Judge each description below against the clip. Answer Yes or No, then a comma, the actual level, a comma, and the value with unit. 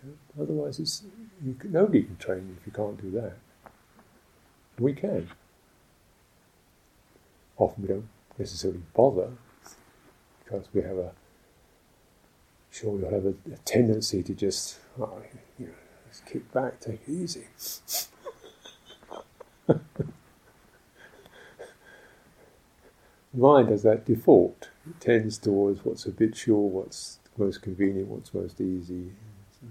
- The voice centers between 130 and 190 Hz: No, low, 105 Hz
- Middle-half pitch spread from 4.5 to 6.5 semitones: Yes, wide, 5.5 semitones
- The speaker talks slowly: Yes, slow, 115 wpm